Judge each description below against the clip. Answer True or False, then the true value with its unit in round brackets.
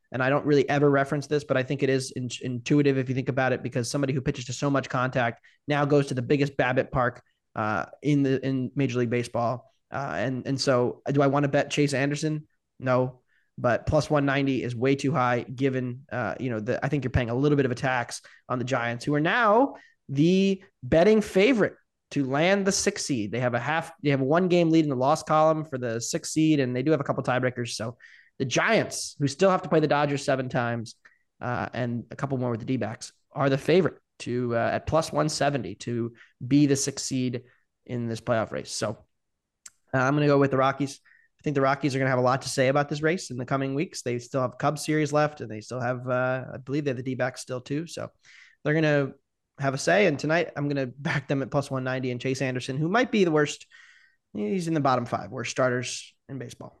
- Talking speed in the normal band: False (245 wpm)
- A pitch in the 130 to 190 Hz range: True (135 Hz)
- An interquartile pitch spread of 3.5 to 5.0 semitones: False (2.8 semitones)